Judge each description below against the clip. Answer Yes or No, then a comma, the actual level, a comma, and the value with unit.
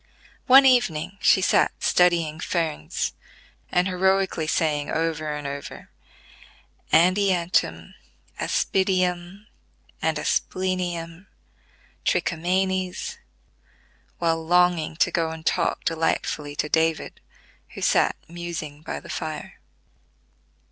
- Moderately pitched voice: Yes, medium, 170 Hz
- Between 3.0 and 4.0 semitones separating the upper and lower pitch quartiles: No, narrow, 2.6 semitones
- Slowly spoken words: Yes, slow, 95 wpm